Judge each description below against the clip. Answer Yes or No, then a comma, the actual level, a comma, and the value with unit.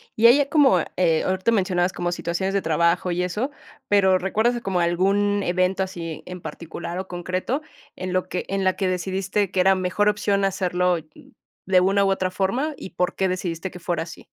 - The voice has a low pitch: No, medium, 185 Hz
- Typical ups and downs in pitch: No, narrow, 1.8 semitones